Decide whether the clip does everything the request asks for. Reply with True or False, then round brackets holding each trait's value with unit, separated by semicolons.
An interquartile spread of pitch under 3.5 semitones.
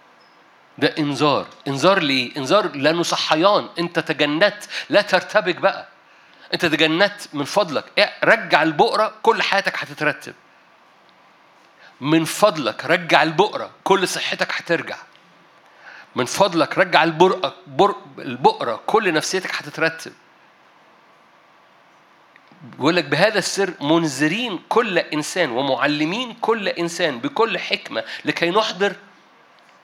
False (4.5 semitones)